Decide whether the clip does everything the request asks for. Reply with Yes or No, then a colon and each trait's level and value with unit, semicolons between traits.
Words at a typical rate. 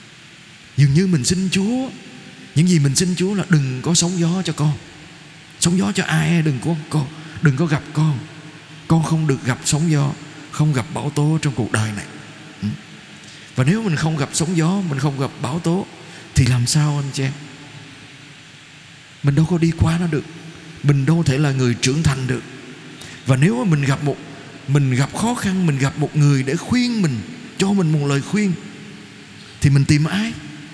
Yes: average, 195 wpm